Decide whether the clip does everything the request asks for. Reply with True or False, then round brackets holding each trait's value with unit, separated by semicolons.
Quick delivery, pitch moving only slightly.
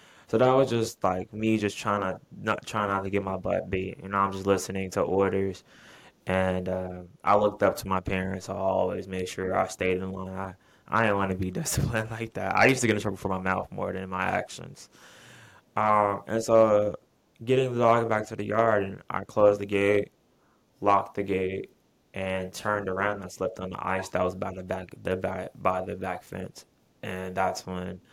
True (220 wpm; 1.9 semitones)